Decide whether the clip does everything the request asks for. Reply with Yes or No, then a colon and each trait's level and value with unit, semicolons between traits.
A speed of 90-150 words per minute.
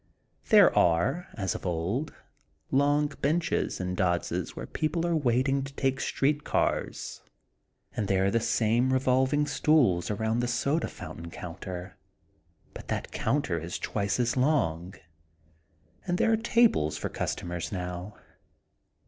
Yes: average, 140 wpm